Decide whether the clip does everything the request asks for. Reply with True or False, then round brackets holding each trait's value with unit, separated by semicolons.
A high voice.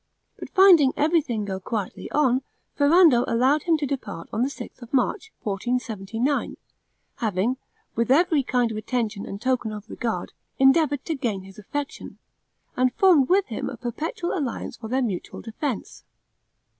True (250 Hz)